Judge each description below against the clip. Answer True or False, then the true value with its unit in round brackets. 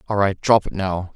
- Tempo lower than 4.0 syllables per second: False (5.0 syllables/s)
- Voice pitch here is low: True (100 Hz)